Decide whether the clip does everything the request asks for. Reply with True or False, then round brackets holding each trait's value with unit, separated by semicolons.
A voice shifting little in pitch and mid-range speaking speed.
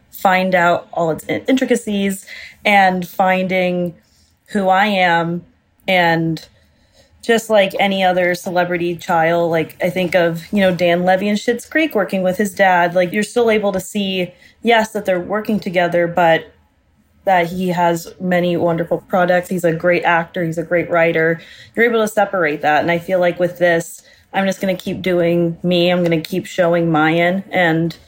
True (2.2 semitones; 175 wpm)